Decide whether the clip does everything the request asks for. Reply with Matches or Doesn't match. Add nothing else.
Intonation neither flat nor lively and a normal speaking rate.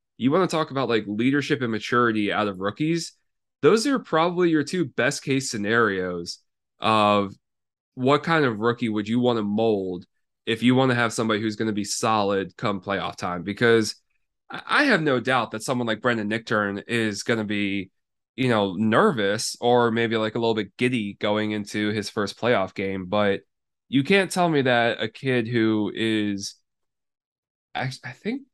Matches